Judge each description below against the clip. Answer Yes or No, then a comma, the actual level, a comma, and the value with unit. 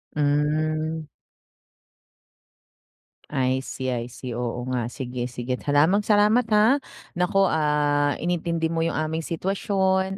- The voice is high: No, medium, 155 Hz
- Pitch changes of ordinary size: No, wide, 6.2 semitones